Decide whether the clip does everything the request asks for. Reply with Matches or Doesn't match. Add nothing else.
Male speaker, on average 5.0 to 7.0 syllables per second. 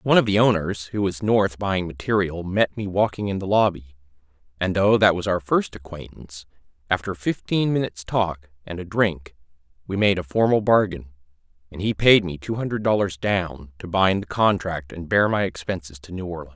Matches